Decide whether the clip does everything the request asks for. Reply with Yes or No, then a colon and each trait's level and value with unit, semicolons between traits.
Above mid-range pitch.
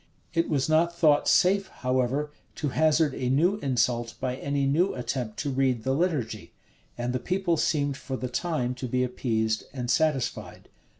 No: low, 135 Hz